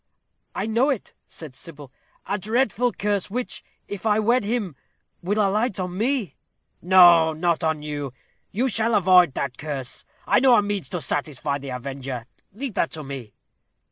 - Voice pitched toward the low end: No, medium, 185 Hz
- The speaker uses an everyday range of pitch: No, wide, 6.6 semitones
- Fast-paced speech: No, average, 165 wpm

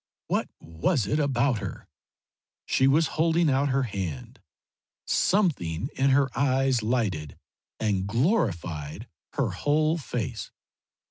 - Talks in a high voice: No, low, 130 Hz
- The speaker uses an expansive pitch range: Yes, wide, 7.0 semitones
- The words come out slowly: Yes, slow, 115 wpm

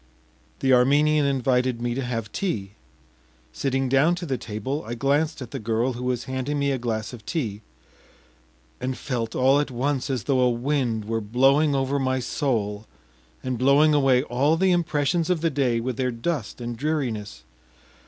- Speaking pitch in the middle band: No, low, 130 Hz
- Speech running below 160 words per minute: No, average, 175 wpm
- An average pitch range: Yes, average, 3.3 semitones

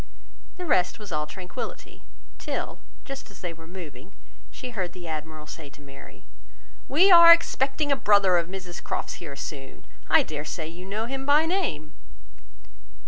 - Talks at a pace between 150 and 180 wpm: Yes, average, 165 wpm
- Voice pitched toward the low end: No, medium, 180 Hz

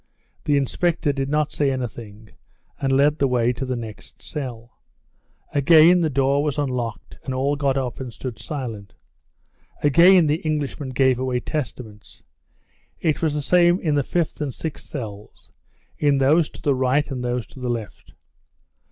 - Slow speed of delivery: No, average, 165 wpm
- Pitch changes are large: No, average, 3.2 semitones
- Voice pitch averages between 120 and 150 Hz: Yes, low, 135 Hz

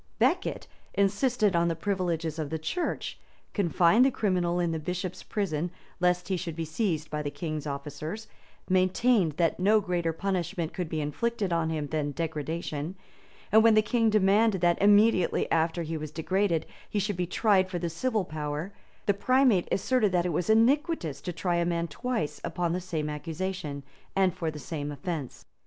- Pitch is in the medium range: Yes, medium, 175 Hz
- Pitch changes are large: No, average, 4.0 semitones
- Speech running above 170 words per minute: Yes, average, 180 wpm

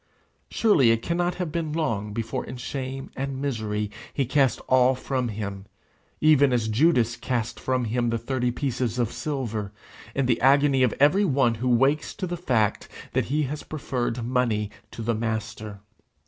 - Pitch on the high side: No, low, 125 Hz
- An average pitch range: Yes, average, 3.6 semitones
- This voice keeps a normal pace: Yes, average, 170 wpm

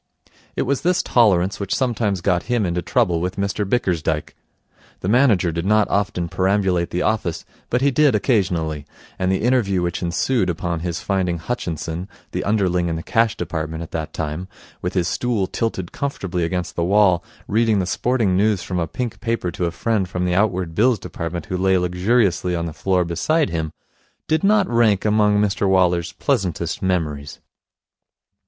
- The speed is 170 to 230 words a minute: Yes, average, 175 wpm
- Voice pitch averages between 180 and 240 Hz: No, very low, 95 Hz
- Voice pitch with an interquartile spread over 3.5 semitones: Yes, average, 4.0 semitones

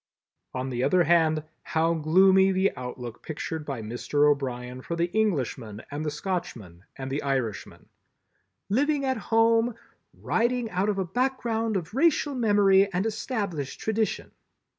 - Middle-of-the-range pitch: Yes, medium, 180 Hz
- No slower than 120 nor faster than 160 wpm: Yes, average, 140 wpm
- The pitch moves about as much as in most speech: No, wide, 7.8 semitones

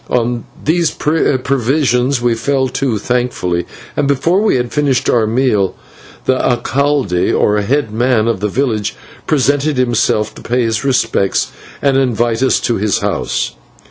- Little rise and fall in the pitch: No, average, 3.5 semitones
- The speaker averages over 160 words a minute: No, average, 150 wpm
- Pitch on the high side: No, low, 125 Hz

